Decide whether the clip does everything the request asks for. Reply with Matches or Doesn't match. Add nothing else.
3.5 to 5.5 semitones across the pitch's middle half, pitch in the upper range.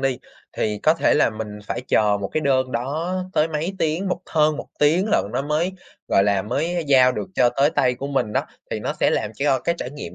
Doesn't match